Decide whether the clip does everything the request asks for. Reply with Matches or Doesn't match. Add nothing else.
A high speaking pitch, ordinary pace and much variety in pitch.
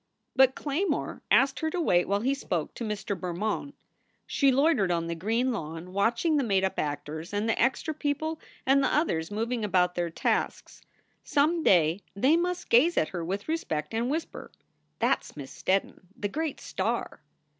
Matches